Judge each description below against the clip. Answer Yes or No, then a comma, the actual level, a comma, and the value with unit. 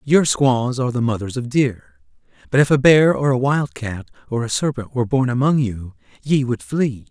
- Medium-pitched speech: No, low, 125 Hz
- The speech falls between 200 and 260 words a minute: Yes, fast, 205 wpm